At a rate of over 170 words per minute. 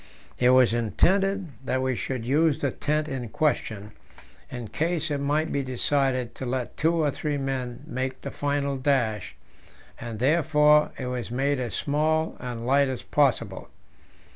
No: average, 160 wpm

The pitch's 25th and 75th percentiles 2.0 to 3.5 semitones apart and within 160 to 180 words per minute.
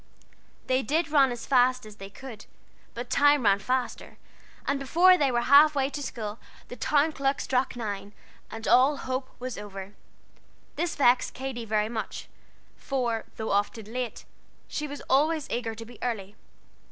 No: average, 3.9 semitones; average, 165 wpm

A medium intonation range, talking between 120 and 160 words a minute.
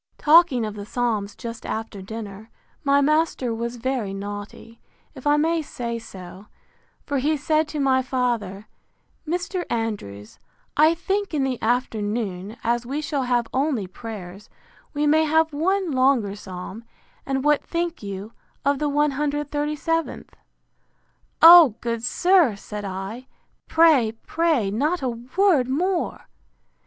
No: wide, 5.8 semitones; slow, 135 wpm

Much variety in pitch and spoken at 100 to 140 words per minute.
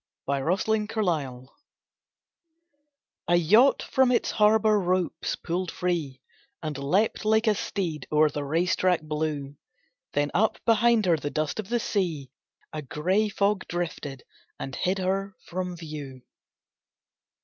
Yes: wide, 5.7 semitones; slow, 135 wpm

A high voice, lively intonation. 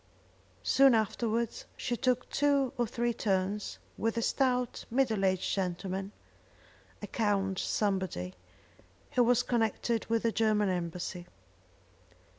No: high, 220 Hz; average, 3.8 semitones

